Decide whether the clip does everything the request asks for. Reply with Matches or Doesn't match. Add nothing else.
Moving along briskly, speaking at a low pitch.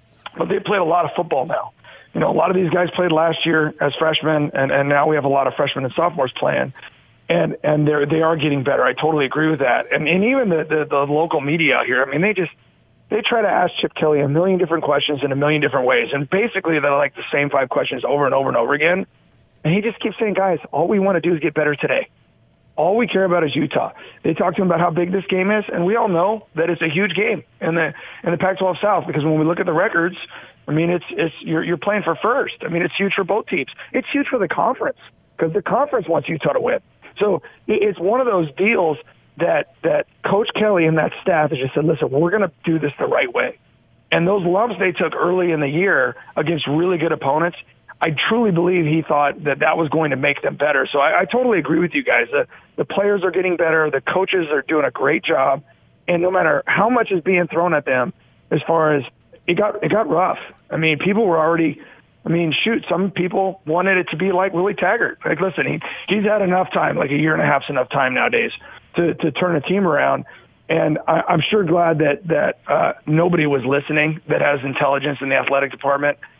Doesn't match